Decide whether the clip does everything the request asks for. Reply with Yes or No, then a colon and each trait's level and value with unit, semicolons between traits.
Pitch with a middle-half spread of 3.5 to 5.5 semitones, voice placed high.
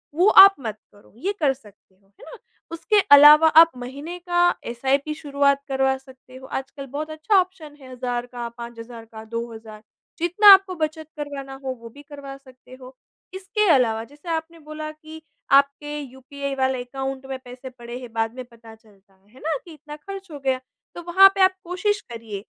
Yes: average, 4.3 semitones; very high, 275 Hz